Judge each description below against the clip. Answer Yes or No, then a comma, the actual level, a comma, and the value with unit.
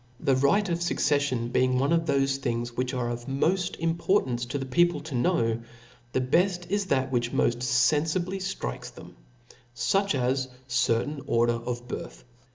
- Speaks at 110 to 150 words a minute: No, average, 170 wpm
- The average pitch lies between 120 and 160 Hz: Yes, low, 135 Hz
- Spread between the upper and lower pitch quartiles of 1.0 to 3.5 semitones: No, wide, 5.5 semitones